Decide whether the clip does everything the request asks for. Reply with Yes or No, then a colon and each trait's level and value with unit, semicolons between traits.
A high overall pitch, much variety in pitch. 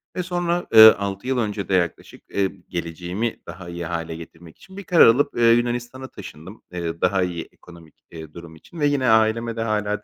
No: low, 105 Hz; wide, 5.9 semitones